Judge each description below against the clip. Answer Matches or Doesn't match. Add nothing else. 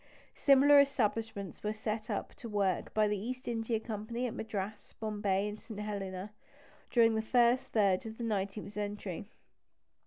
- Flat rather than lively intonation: Matches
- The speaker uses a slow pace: Doesn't match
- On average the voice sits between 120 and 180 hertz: Doesn't match